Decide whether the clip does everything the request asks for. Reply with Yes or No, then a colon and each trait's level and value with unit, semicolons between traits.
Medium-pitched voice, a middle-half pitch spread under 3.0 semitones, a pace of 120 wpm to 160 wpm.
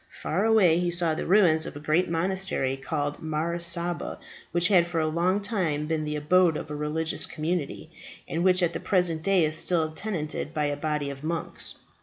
No: medium, 165 Hz; narrow, 2.6 semitones; average, 200 wpm